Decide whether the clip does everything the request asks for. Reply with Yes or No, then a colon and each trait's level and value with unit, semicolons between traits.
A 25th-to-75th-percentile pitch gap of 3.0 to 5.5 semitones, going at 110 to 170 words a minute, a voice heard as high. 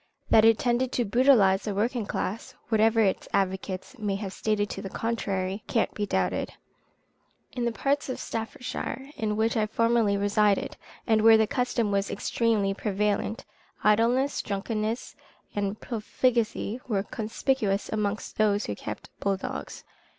No: narrow, 2.6 semitones; average, 145 wpm; high, 215 Hz